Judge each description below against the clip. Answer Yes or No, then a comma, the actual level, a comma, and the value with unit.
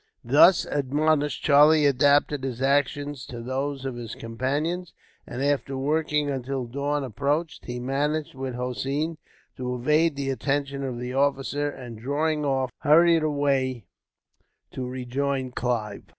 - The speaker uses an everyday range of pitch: No, narrow, 2.3 semitones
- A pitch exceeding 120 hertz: Yes, medium, 140 Hz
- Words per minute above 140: No, slow, 135 wpm